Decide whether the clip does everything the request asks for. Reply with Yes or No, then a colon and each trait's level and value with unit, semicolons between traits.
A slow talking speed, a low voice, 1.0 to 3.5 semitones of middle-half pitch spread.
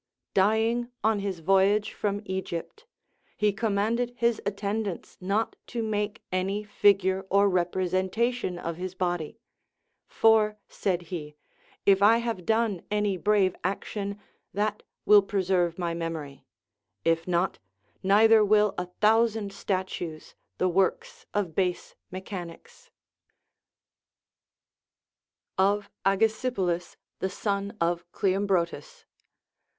No: slow, 105 wpm; high, 200 Hz; narrow, 2.6 semitones